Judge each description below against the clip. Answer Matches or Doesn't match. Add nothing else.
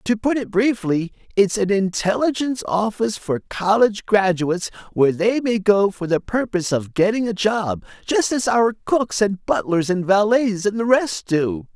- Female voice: Doesn't match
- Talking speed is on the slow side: Doesn't match